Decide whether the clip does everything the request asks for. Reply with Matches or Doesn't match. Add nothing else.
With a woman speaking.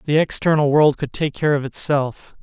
Doesn't match